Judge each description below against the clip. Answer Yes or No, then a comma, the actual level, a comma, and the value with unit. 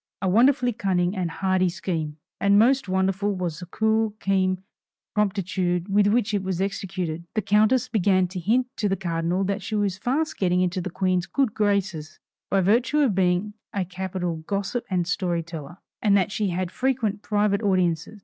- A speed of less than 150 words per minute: No, average, 180 wpm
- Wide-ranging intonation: No, narrow, 2.6 semitones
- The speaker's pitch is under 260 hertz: Yes, high, 190 Hz